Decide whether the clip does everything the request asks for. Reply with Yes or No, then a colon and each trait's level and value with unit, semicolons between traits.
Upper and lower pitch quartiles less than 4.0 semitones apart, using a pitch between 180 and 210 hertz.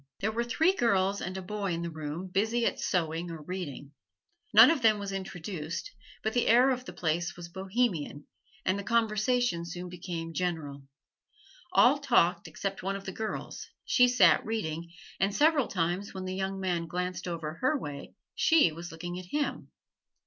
No: average, 4.6 semitones; medium, 185 Hz